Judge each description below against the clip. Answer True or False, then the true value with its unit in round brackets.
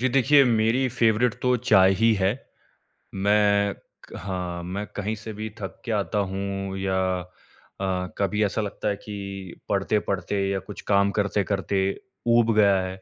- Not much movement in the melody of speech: True (2.2 semitones)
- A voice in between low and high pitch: False (100 Hz)